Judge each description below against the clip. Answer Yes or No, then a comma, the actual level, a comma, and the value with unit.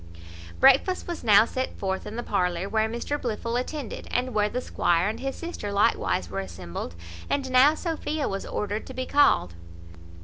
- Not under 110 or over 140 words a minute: No, average, 175 wpm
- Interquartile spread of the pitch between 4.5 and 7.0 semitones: Yes, average, 5.3 semitones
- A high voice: Yes, high, 230 Hz